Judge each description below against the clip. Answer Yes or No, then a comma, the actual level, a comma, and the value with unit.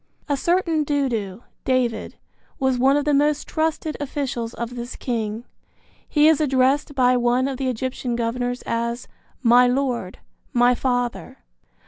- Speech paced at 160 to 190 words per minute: No, average, 140 wpm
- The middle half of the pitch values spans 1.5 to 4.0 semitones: Yes, average, 2.8 semitones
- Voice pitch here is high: Yes, very high, 255 Hz